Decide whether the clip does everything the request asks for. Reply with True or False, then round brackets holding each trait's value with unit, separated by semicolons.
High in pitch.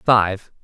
False (105 Hz)